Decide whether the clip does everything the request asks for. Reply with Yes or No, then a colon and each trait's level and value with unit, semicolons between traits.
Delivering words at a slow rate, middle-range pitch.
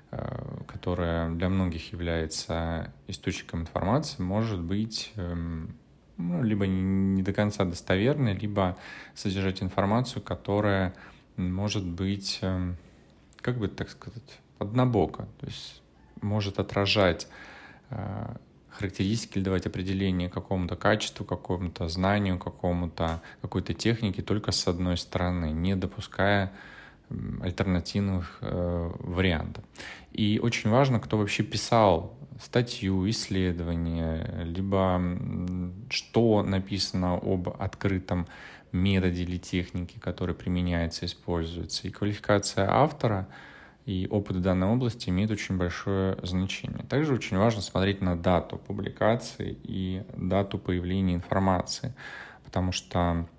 No: slow, 105 wpm; very low, 95 Hz